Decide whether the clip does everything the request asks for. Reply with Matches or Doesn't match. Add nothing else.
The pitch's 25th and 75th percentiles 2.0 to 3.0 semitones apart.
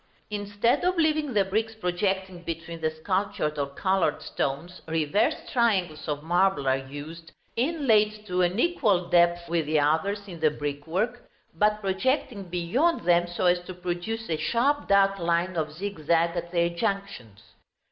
Doesn't match